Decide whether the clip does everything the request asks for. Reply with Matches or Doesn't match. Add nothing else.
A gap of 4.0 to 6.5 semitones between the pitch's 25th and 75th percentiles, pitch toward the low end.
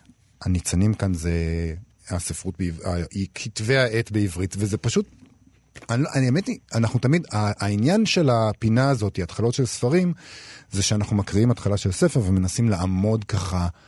Matches